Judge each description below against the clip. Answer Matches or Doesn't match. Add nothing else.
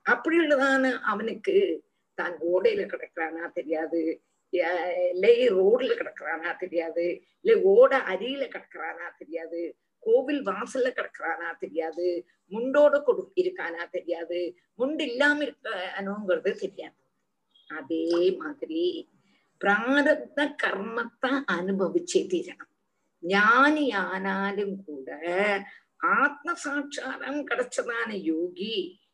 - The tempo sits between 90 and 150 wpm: Doesn't match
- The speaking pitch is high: Matches